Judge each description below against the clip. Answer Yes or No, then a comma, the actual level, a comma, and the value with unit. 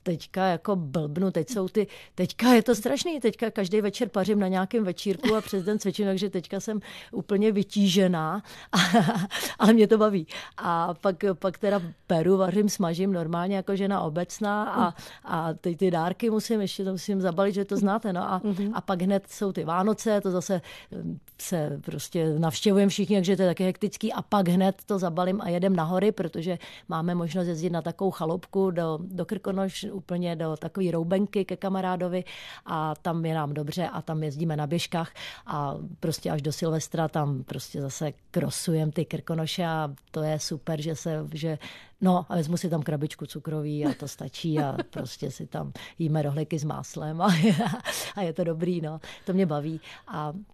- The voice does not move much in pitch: No, average, 3.4 semitones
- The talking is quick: Yes, fast, 180 wpm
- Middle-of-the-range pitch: Yes, medium, 180 Hz